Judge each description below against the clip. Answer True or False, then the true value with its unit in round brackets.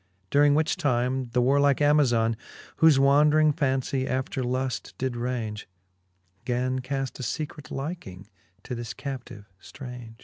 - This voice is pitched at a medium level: False (130 Hz)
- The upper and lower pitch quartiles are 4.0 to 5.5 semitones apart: False (2.7 semitones)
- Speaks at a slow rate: True (130 wpm)